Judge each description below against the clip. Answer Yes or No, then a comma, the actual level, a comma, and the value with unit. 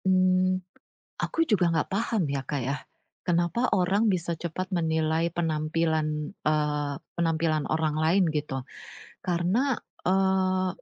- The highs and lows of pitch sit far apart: No, average, 3.2 semitones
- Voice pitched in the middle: Yes, medium, 170 Hz